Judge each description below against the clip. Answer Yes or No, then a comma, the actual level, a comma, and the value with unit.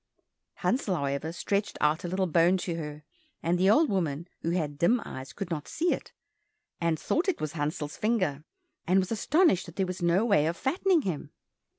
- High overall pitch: No, medium, 175 Hz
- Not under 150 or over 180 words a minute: No, average, 195 wpm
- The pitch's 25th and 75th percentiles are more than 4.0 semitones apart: Yes, average, 4.7 semitones